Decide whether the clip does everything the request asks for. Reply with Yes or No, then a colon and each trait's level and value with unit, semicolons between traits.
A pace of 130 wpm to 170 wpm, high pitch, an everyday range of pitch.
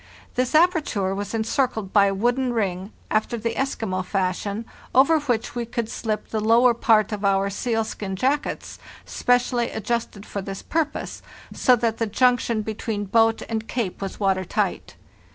Yes: average, 155 wpm; high, 225 Hz; average, 3.4 semitones